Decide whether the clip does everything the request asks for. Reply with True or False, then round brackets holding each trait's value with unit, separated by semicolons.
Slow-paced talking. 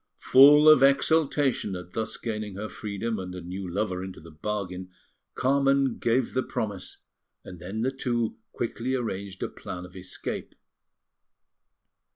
False (145 wpm)